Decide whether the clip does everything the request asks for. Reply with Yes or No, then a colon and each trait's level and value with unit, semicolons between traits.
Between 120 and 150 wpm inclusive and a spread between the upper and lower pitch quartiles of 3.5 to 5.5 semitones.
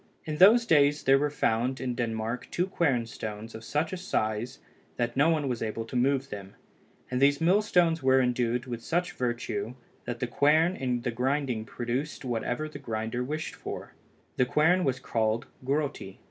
No: average, 175 wpm; average, 4.2 semitones